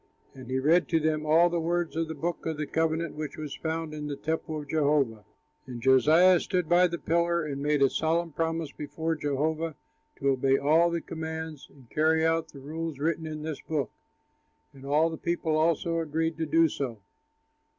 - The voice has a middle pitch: Yes, medium, 160 Hz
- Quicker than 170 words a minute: Yes, average, 195 wpm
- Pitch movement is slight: Yes, narrow, 2.0 semitones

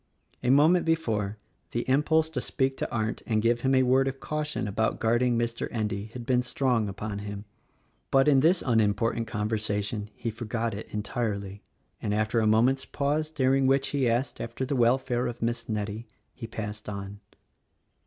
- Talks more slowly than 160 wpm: No, average, 180 wpm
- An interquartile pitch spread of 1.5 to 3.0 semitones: No, average, 3.7 semitones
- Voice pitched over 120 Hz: No, low, 115 Hz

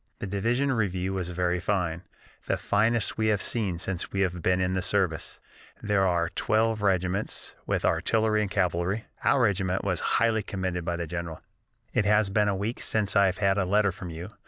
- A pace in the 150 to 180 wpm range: No, average, 195 wpm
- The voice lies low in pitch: Yes, very low, 95 Hz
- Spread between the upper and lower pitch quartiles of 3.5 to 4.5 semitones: No, average, 2.8 semitones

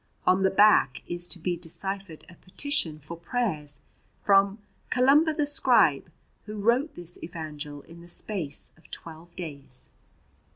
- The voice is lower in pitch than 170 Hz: No, medium, 175 Hz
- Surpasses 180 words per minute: No, average, 140 wpm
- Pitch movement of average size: Yes, average, 4.6 semitones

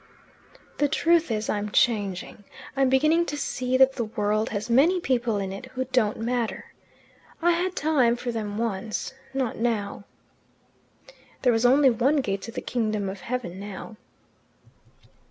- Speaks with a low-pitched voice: No, high, 235 Hz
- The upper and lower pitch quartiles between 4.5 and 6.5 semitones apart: No, average, 4.1 semitones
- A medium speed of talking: Yes, average, 155 wpm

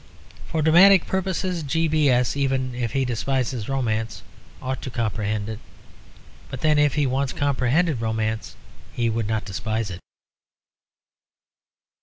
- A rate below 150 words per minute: Yes, slow, 135 wpm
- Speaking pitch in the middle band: No, low, 130 Hz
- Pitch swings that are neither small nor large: Yes, average, 4.8 semitones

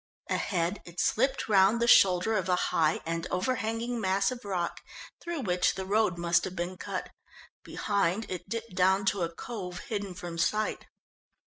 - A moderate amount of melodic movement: Yes, average, 3.6 semitones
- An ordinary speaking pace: Yes, average, 170 wpm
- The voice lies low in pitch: No, high, 190 Hz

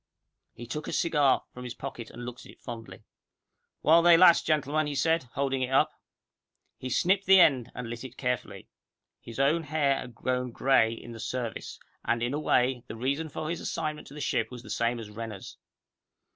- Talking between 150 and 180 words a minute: No, average, 200 wpm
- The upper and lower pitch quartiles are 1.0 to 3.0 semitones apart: No, average, 4.2 semitones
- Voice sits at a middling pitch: No, low, 130 Hz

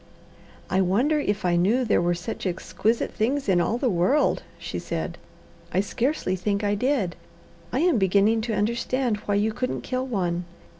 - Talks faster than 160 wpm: Yes, average, 170 wpm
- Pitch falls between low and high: No, high, 210 Hz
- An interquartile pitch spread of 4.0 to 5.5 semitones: Yes, average, 5.1 semitones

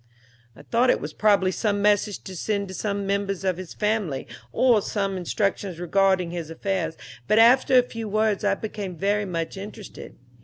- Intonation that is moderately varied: No, narrow, 2.2 semitones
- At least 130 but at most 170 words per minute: No, average, 180 wpm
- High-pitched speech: Yes, high, 200 Hz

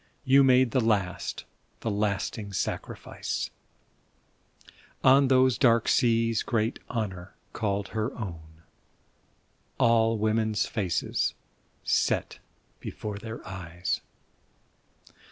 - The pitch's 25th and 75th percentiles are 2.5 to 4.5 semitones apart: Yes, average, 2.8 semitones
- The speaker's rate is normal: No, slow, 90 wpm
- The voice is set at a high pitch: No, low, 110 Hz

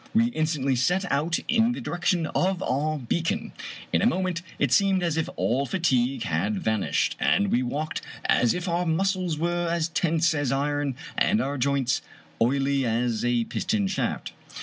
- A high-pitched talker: No, medium, 155 Hz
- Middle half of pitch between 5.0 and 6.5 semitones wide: Yes, wide, 5.4 semitones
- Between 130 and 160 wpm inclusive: No, average, 170 wpm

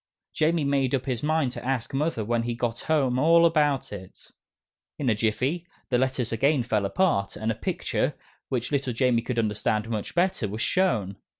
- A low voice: Yes, low, 125 Hz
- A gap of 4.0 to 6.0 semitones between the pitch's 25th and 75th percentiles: Yes, average, 4.6 semitones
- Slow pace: No, average, 185 wpm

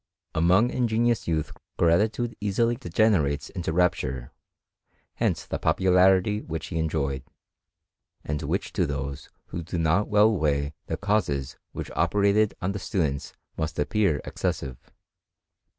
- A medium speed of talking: No, slow, 125 wpm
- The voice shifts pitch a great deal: Yes, wide, 5.7 semitones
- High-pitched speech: No, very low, 90 Hz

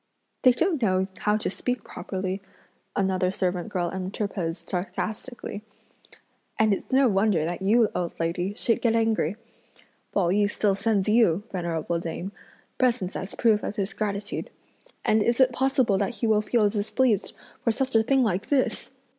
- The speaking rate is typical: Yes, average, 165 wpm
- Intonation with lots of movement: No, average, 3.6 semitones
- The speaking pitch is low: No, high, 205 Hz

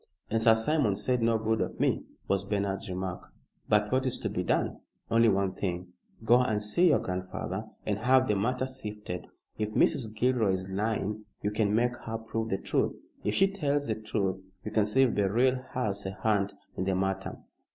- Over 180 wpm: Yes, average, 195 wpm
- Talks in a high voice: No, low, 110 Hz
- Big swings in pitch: No, average, 3.6 semitones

